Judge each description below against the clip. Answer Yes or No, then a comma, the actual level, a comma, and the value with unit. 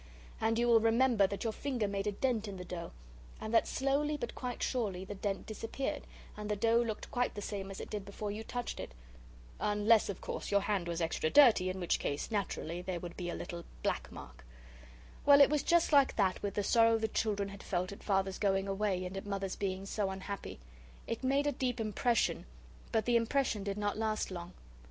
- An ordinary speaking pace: No, fast, 215 wpm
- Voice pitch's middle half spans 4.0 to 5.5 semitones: No, average, 3.1 semitones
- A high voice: Yes, high, 205 Hz